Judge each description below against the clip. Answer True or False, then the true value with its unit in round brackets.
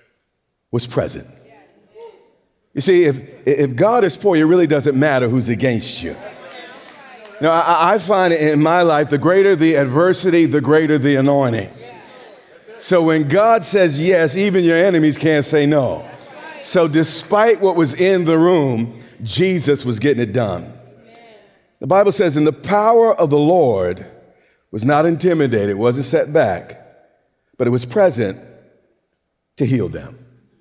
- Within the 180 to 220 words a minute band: False (150 wpm)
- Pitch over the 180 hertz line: False (155 Hz)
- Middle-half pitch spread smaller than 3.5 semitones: False (5.3 semitones)